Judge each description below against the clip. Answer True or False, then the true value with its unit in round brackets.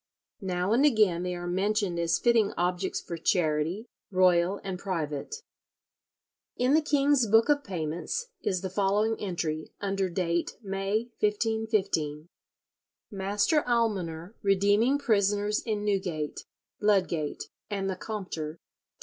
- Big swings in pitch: False (3.7 semitones)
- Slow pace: True (125 wpm)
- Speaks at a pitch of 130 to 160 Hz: False (195 Hz)